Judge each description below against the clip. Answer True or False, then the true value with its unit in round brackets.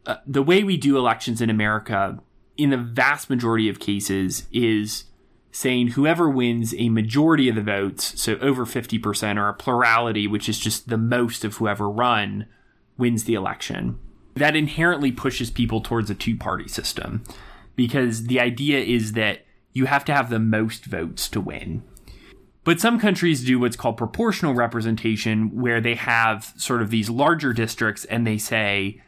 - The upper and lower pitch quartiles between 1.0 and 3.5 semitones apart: True (3.0 semitones)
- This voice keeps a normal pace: True (165 wpm)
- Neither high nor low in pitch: False (115 Hz)